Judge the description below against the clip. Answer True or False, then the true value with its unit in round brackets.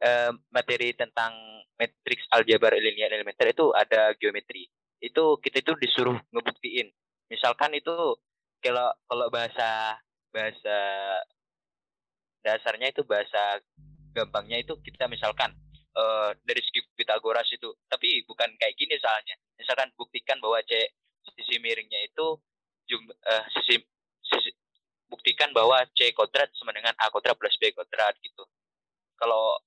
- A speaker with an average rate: True (125 wpm)